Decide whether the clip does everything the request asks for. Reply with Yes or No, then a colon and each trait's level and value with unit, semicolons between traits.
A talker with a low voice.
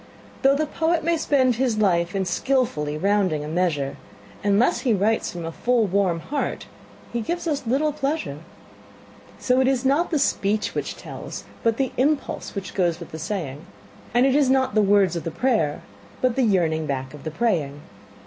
No: high, 210 Hz